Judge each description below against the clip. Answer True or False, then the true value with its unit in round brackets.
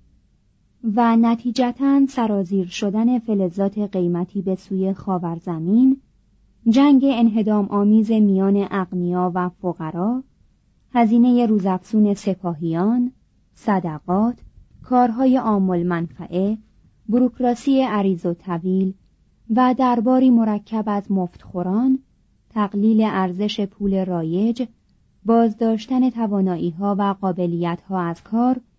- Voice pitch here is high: True (205 Hz)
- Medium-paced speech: False (95 wpm)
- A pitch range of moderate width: True (4.3 semitones)